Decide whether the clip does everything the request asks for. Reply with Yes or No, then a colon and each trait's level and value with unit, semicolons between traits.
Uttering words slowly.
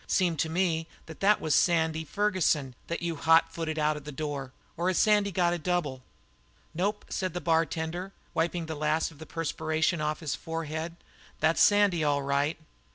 No: average, 180 wpm